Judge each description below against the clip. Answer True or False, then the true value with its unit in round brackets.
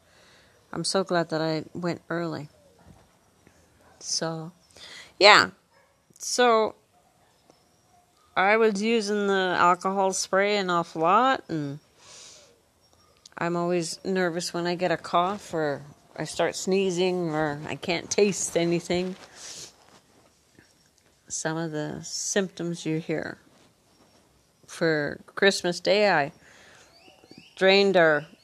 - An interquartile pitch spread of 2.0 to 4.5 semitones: True (2.9 semitones)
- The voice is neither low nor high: True (175 Hz)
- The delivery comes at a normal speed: False (105 wpm)